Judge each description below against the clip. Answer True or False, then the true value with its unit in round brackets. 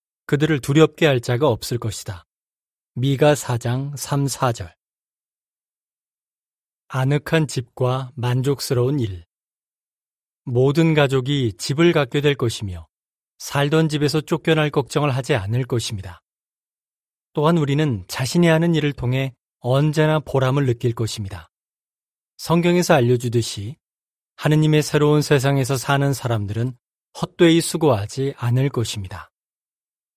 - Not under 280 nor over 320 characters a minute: False (250 characters per minute)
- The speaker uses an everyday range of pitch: True (3.9 semitones)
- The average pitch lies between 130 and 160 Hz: True (135 Hz)